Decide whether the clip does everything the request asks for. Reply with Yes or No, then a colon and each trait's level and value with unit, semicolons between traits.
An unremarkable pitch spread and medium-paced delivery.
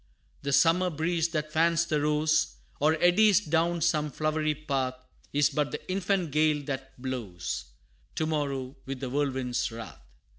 Yes: average, 3.2 semitones; average, 150 wpm